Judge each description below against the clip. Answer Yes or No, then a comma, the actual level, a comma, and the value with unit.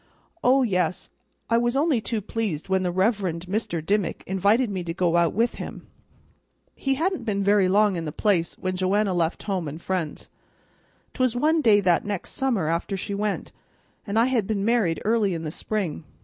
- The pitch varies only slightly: No, average, 4.2 semitones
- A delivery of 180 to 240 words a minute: Yes, average, 190 wpm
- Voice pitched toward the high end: Yes, high, 200 Hz